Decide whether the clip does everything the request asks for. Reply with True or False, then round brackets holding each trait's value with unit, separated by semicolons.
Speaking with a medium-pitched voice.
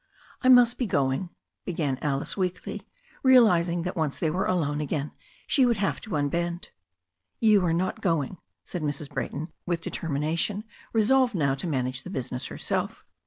True (170 Hz)